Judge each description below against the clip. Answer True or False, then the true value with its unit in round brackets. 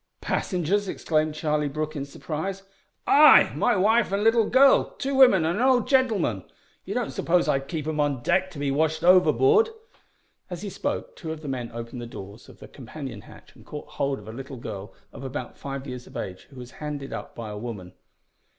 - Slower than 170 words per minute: False (205 wpm)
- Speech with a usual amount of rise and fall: False (6.7 semitones)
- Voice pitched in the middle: True (150 Hz)